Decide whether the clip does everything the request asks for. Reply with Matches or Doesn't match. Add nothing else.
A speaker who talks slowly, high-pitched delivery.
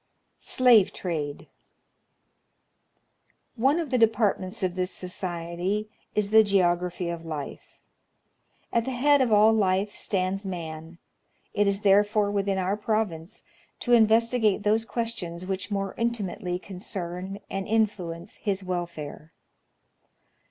Matches